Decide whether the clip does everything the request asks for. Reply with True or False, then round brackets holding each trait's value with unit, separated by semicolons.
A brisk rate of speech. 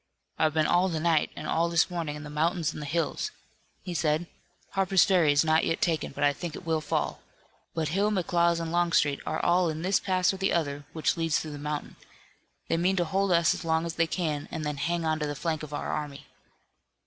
True (230 wpm)